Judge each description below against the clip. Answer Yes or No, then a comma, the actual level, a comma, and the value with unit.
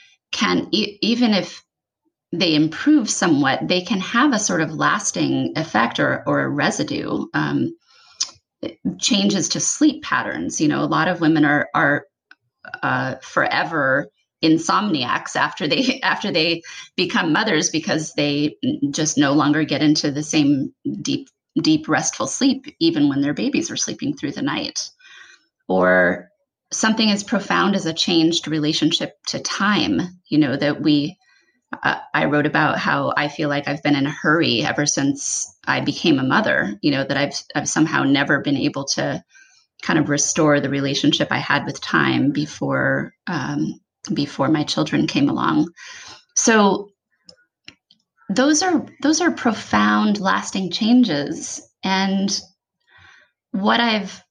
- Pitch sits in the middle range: Yes, medium, 180 Hz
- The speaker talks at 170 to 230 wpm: No, average, 145 wpm